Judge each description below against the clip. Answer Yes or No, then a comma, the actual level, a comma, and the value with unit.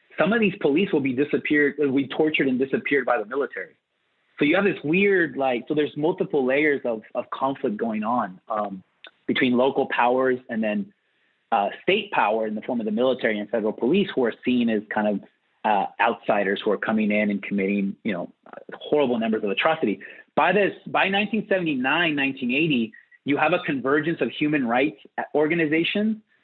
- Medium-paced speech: Yes, average, 185 wpm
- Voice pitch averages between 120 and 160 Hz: Yes, low, 135 Hz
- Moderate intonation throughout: No, wide, 6.7 semitones